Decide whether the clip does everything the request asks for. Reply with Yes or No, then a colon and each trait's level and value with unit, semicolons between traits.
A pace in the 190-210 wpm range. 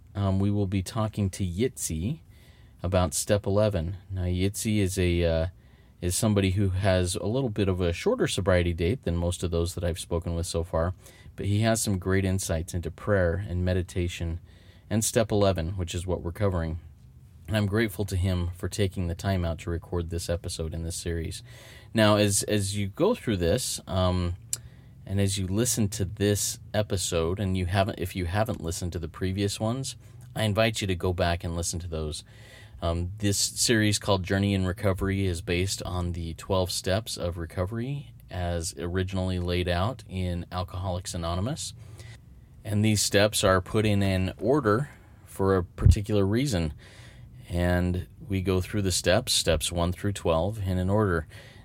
No: average, 180 wpm